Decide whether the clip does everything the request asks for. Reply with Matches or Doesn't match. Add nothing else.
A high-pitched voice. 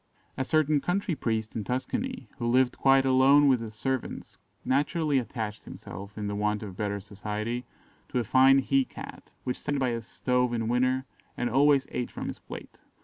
Doesn't match